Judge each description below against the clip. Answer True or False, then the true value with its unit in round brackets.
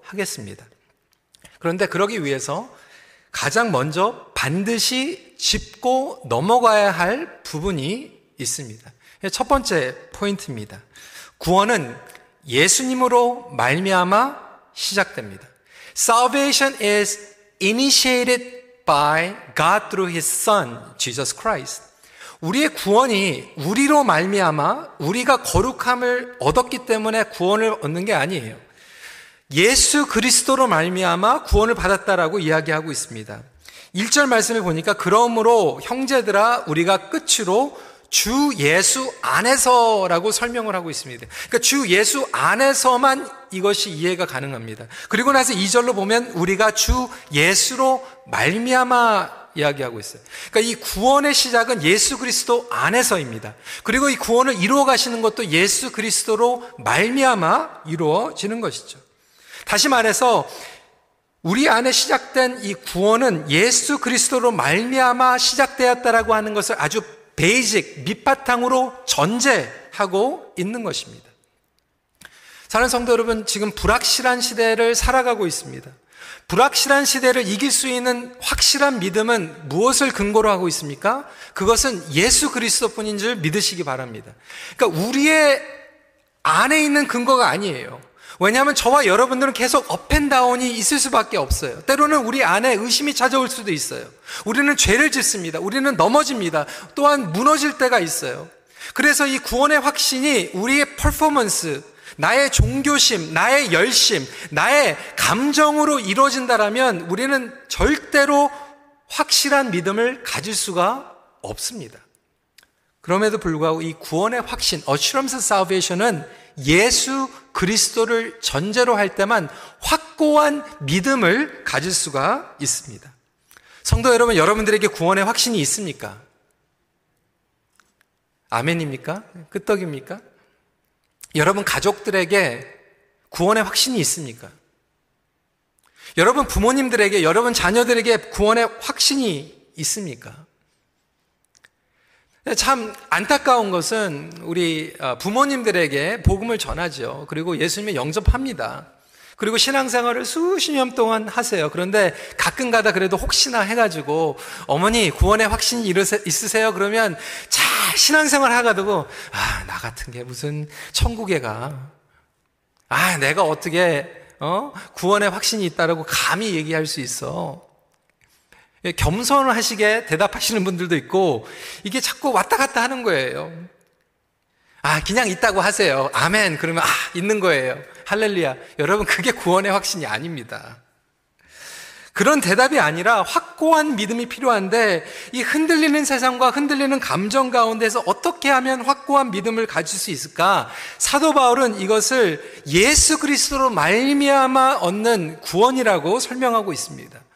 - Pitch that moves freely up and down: True (5.8 semitones)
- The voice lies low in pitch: False (225 Hz)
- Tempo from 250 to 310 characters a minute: True (305 characters per minute)